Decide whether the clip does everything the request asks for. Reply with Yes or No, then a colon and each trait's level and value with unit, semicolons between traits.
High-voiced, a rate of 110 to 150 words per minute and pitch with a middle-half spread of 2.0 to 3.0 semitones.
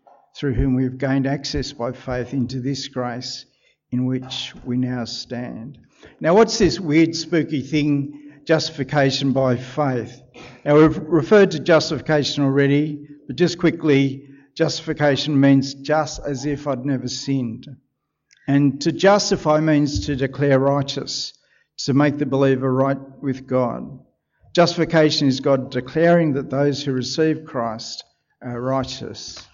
No: medium, 140 Hz; slow, 135 wpm; narrow, 2.6 semitones